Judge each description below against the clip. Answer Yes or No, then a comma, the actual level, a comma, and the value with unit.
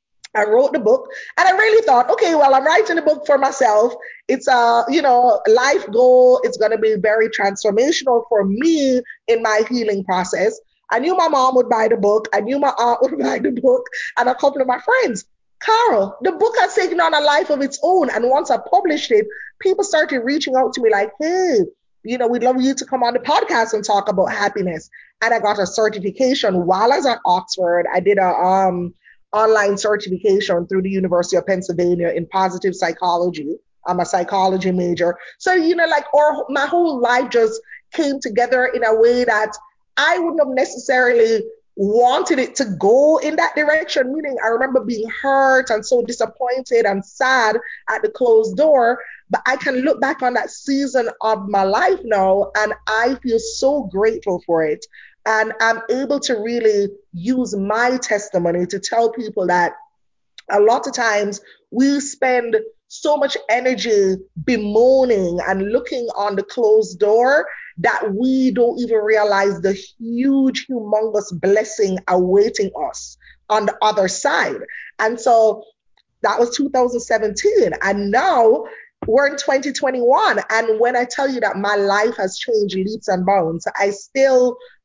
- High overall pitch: Yes, high, 235 Hz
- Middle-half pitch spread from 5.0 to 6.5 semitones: Yes, wide, 5.4 semitones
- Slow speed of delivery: No, average, 175 wpm